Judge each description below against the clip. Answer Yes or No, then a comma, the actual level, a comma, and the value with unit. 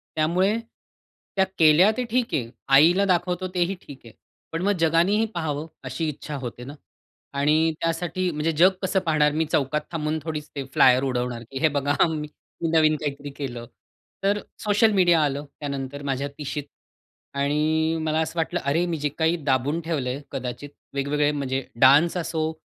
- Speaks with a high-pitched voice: No, medium, 155 Hz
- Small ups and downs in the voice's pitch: No, average, 3.2 semitones